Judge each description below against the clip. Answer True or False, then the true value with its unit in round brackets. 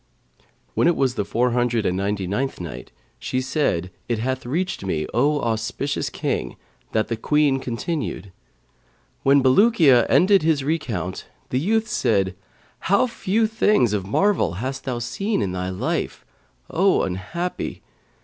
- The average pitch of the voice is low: True (130 Hz)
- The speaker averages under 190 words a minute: True (145 wpm)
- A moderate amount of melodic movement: False (7.9 semitones)